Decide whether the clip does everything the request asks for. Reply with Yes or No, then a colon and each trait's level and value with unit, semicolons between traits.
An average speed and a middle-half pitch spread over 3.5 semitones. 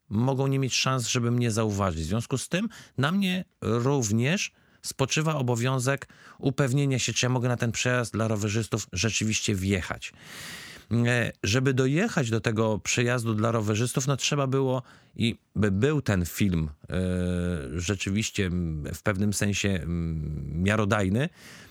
Yes: average, 135 wpm; average, 4.7 semitones